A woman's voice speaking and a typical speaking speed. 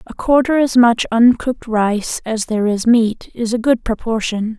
Yes: female; average, 185 wpm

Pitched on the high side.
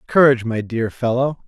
No: low, 120 Hz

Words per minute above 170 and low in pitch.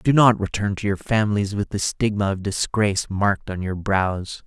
Yes: average, 200 wpm; low, 100 Hz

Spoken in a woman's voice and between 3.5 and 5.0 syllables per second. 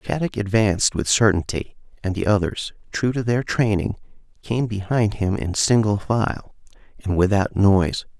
No: male; 4.7 syllables/s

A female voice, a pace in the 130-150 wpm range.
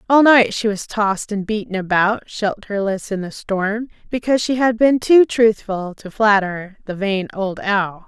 No: female; average, 180 wpm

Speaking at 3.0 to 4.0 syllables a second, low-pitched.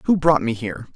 No: 6.8 syllables/s; low, 130 Hz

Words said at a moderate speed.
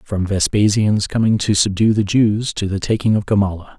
Yes: average, 190 wpm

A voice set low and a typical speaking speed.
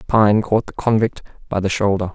Yes: low, 105 Hz; average, 195 wpm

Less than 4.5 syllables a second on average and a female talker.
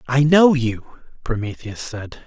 No: 3.8 syllables/s; male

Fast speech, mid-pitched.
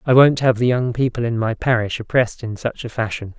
No: fast, 250 wpm; low, 120 Hz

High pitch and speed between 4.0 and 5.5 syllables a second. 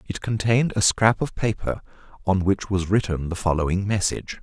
No: low, 100 Hz; 5.4 syllables/s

